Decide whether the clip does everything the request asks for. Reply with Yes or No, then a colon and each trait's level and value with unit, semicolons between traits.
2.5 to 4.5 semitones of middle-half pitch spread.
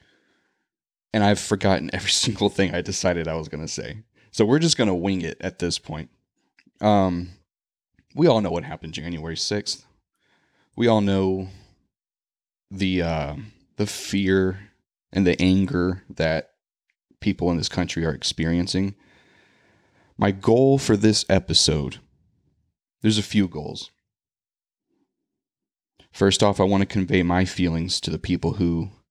Yes: average, 2.8 semitones